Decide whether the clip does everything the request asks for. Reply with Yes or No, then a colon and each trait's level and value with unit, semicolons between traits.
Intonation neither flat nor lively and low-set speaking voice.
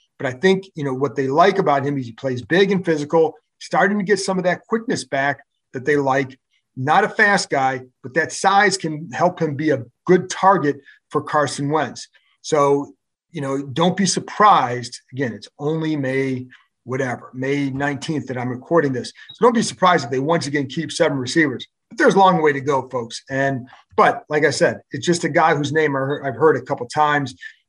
No: average, 4.0 semitones; medium, 145 Hz